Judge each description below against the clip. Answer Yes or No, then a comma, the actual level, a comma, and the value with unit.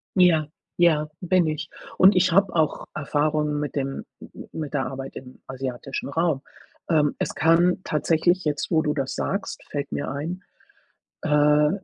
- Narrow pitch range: No, average, 3.0 semitones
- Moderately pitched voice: Yes, medium, 150 Hz